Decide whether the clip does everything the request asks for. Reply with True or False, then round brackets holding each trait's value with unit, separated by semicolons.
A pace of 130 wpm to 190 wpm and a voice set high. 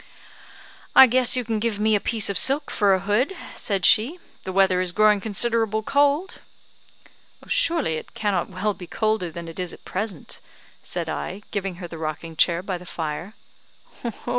True (175 wpm; 205 Hz)